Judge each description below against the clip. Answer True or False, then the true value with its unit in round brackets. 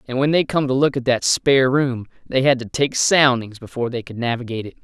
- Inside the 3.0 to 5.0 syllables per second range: False (6.0 syllables/s)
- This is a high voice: False (130 Hz)